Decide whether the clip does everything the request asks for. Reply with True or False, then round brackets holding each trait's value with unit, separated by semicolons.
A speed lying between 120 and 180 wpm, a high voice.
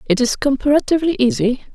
True (140 wpm; 270 Hz)